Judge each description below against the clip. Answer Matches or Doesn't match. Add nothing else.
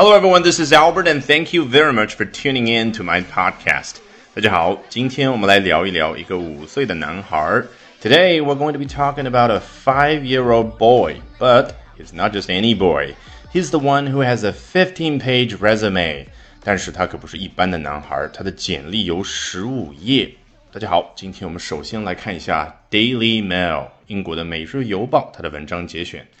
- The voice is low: Matches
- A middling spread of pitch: Doesn't match